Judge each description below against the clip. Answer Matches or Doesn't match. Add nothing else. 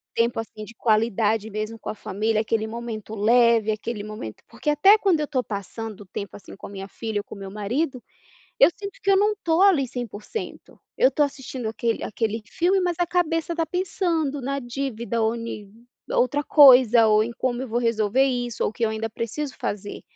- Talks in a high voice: Matches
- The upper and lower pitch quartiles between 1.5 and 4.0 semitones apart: Doesn't match